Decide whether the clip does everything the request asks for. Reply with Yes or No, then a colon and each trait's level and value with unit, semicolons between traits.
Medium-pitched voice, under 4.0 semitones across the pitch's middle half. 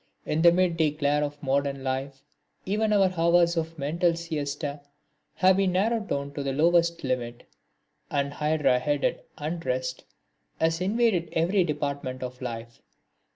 Yes: medium, 150 Hz; average, 3.6 semitones